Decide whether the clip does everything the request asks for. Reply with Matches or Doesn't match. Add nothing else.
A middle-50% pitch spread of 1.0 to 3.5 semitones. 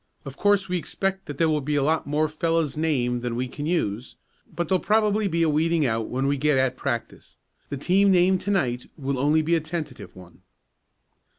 Doesn't match